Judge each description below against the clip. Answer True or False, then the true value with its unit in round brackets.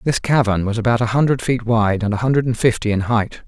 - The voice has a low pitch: True (115 Hz)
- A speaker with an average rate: False (260 wpm)